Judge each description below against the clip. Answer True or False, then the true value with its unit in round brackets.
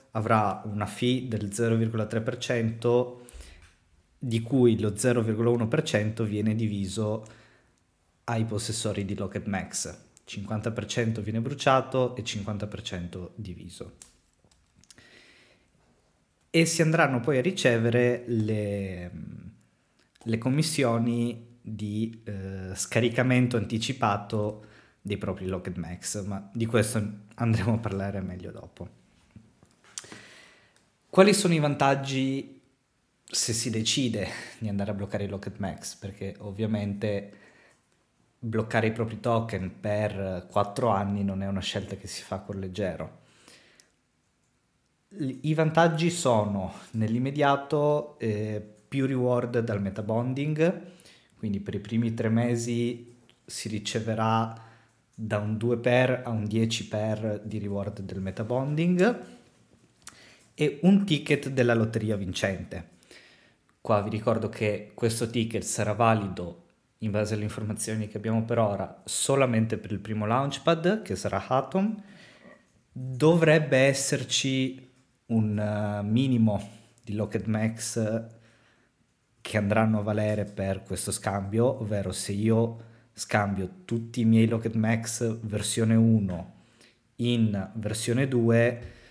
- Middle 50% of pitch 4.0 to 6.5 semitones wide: False (2.7 semitones)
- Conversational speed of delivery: False (110 wpm)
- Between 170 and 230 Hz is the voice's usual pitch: False (110 Hz)